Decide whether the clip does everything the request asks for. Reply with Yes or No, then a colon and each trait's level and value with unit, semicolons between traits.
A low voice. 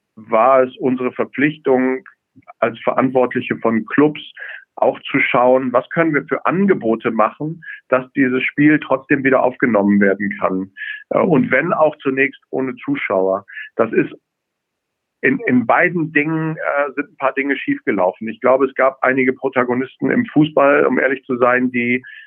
Yes: low, 130 Hz